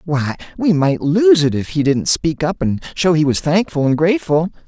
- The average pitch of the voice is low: No, medium, 160 Hz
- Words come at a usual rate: No, fast, 220 wpm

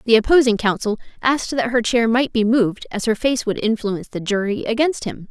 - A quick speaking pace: Yes, fast, 215 wpm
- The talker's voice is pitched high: Yes, high, 225 Hz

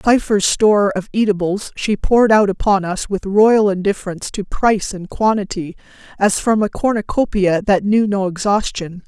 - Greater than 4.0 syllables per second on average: Yes, 5.0 syllables/s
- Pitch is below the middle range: No, high, 200 Hz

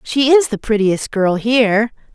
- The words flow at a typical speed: Yes, average, 170 wpm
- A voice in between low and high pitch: No, high, 225 Hz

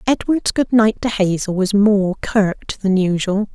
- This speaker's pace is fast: No, average, 170 wpm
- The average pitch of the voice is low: No, high, 205 Hz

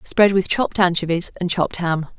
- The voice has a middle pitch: Yes, medium, 180 Hz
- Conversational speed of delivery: Yes, average, 190 wpm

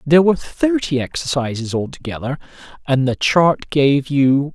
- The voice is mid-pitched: Yes, medium, 145 Hz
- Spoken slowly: Yes, slow, 130 wpm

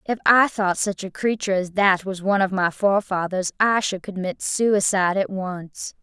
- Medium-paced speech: Yes, average, 190 wpm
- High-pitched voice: Yes, high, 195 Hz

